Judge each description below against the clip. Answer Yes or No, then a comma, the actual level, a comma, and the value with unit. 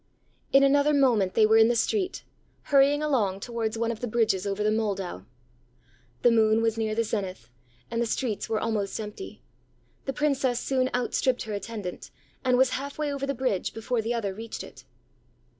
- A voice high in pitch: Yes, high, 230 Hz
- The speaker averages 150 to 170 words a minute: No, average, 190 wpm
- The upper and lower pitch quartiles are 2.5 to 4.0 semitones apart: Yes, average, 3.7 semitones